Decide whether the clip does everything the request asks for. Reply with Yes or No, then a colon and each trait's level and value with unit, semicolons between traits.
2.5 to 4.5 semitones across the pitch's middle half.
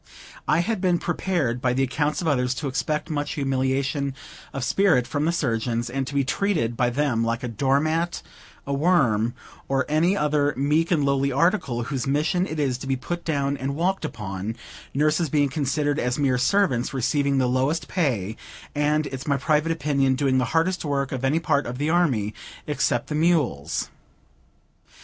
Yes: average, 3.4 semitones